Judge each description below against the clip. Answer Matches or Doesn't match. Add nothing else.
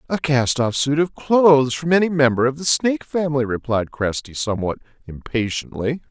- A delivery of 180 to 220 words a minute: Doesn't match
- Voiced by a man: Matches